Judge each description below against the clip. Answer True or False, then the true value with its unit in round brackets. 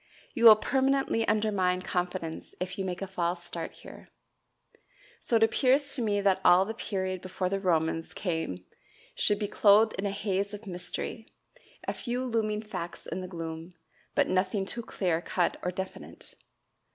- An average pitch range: True (3.3 semitones)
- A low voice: False (190 Hz)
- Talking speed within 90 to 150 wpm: False (165 wpm)